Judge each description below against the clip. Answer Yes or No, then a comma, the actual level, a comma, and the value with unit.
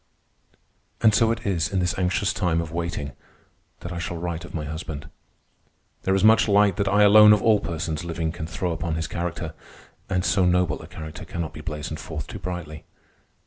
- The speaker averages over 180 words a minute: Yes, average, 195 wpm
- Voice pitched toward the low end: Yes, very low, 85 Hz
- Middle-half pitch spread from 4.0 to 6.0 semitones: No, average, 3.1 semitones